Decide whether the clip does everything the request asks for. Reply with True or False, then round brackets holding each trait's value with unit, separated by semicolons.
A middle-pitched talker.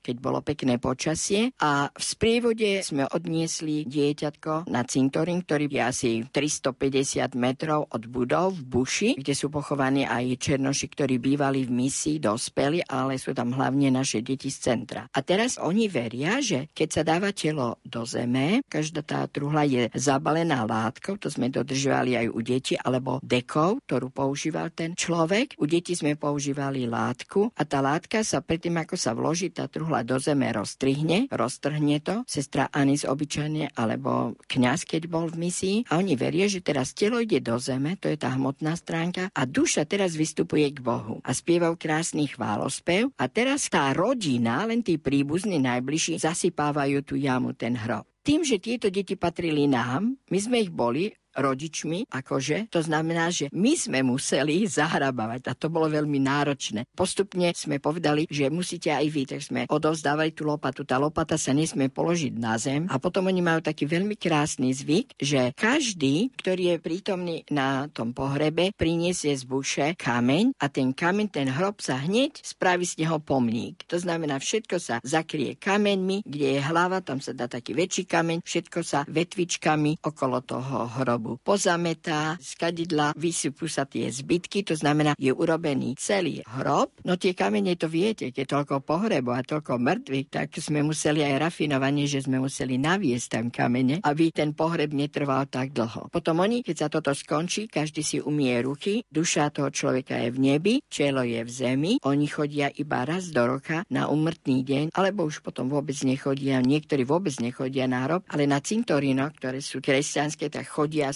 True (150 Hz)